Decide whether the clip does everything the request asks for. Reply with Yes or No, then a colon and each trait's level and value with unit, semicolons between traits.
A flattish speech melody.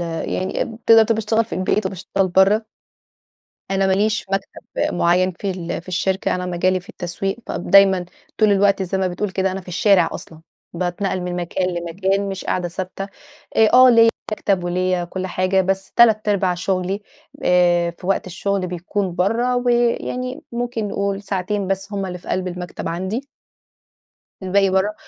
Yes: narrow, 2.0 semitones